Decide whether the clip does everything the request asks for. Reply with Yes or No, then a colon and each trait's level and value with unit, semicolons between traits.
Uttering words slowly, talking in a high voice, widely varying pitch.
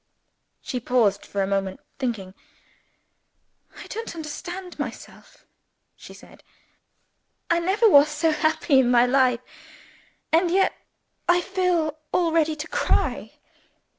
Yes: slow, 120 wpm; very high, 310 Hz; wide, 5.9 semitones